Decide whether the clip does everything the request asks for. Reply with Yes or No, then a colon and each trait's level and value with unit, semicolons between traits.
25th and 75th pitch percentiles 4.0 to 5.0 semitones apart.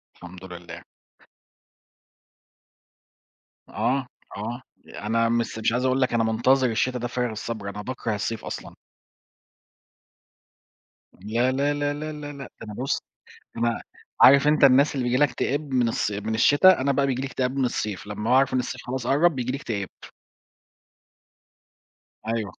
No: average, 3.4 semitones